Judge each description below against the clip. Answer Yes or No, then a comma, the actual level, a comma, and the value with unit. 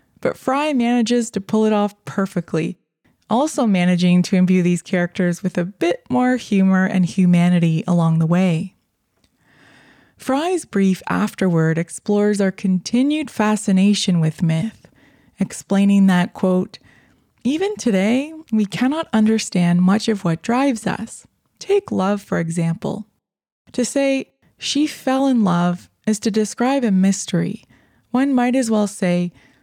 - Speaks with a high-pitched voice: Yes, high, 200 Hz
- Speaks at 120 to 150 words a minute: Yes, slow, 135 wpm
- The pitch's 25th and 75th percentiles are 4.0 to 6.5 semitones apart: Yes, average, 5.1 semitones